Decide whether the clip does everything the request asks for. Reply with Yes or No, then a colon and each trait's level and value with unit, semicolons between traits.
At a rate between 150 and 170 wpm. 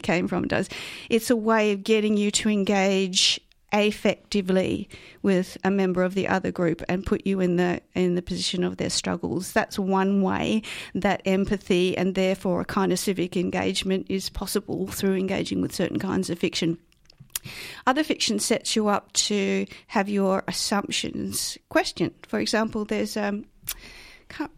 Yes: average, 160 wpm